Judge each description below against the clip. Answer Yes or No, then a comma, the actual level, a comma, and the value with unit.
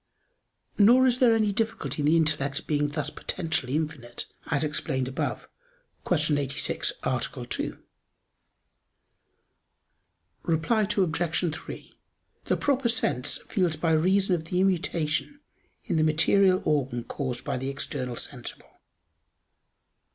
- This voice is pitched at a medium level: Yes, medium, 160 Hz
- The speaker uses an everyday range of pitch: Yes, average, 4.9 semitones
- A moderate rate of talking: No, slow, 120 wpm